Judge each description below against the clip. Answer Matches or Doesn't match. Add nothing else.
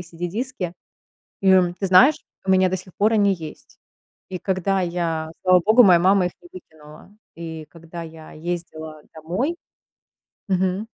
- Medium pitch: Matches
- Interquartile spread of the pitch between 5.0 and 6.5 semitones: Doesn't match